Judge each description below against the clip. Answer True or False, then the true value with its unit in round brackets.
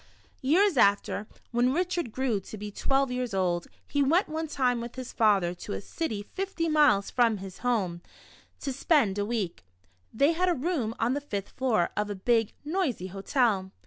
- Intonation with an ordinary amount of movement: False (6.1 semitones)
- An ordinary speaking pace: True (180 wpm)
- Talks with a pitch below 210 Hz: False (240 Hz)